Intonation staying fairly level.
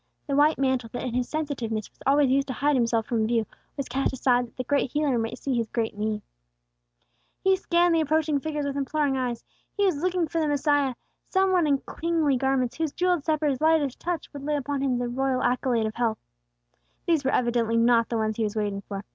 No: average, 4.1 semitones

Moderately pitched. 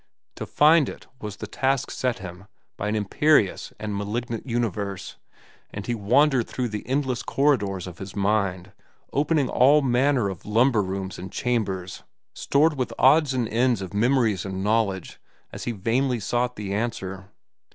No: low, 115 Hz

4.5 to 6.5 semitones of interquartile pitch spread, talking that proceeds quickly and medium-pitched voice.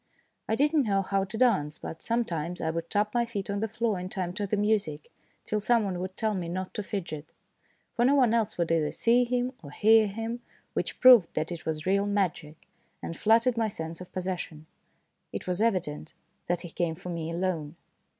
No: average, 4.9 semitones; fast, 215 wpm; high, 195 Hz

